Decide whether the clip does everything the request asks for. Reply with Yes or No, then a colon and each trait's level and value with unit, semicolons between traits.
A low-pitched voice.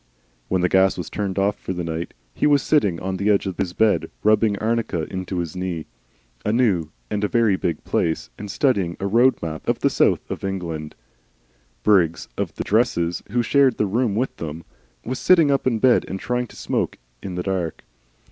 Yes: low, 100 Hz